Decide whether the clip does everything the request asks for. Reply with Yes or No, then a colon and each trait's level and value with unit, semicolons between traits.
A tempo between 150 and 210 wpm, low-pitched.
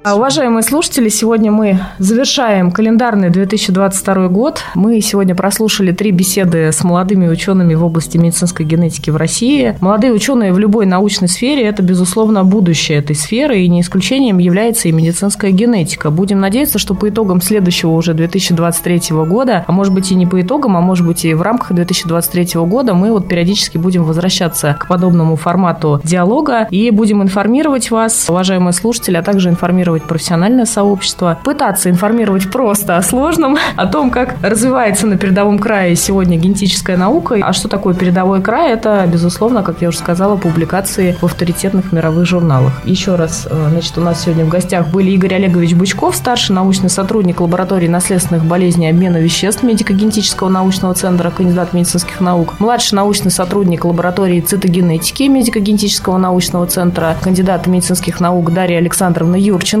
No: average, 155 wpm; medium, 185 Hz